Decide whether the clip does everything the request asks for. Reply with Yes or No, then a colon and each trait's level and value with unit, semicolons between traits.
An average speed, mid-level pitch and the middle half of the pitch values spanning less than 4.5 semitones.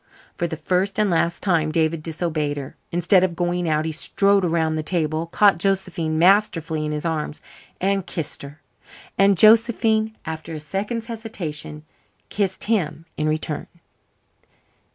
Yes: average, 150 wpm; medium, 170 Hz; average, 3.9 semitones